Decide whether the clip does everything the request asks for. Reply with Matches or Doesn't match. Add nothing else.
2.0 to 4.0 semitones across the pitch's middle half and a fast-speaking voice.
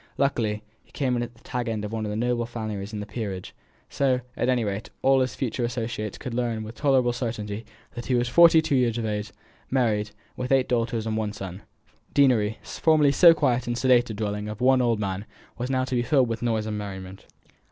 Matches